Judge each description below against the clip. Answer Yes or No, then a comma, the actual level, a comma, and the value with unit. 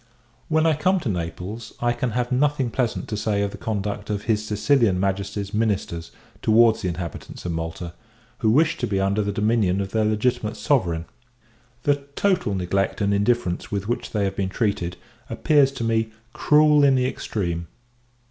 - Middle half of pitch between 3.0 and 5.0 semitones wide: Yes, average, 3.9 semitones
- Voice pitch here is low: Yes, low, 105 Hz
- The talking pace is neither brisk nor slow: Yes, average, 175 wpm